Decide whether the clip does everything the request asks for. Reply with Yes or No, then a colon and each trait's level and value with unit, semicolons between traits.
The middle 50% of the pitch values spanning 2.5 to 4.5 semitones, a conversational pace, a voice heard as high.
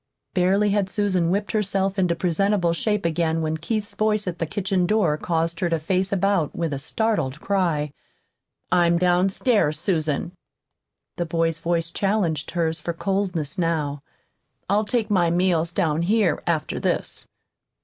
No: average, 3.3 semitones; average, 150 wpm; medium, 175 Hz